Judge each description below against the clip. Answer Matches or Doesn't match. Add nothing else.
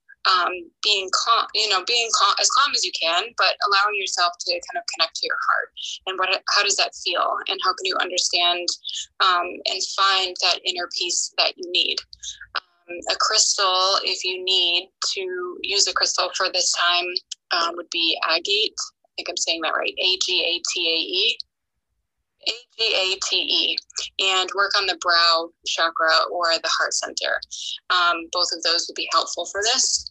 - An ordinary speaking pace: Matches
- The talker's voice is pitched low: Doesn't match